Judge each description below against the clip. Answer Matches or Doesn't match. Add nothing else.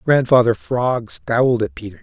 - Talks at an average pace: Matches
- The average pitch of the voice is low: Matches